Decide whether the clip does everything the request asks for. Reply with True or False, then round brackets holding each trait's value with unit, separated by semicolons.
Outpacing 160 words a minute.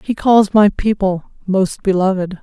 False (150 wpm)